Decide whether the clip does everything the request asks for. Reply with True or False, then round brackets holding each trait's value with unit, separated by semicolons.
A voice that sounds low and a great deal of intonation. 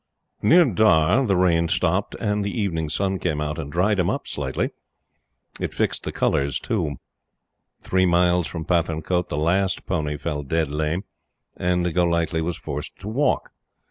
False (85 Hz; 3.4 semitones)